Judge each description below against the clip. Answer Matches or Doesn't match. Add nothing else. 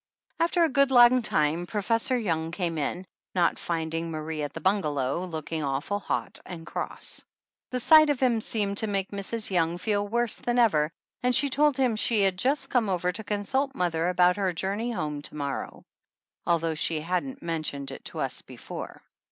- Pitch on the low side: Doesn't match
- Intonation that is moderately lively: Doesn't match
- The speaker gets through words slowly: Doesn't match